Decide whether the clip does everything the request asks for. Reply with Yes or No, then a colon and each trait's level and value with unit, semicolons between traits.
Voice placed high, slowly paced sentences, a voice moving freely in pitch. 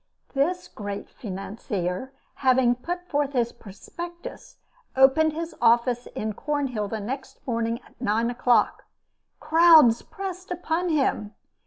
Yes: very high, 260 Hz; slow, 115 wpm; wide, 5.9 semitones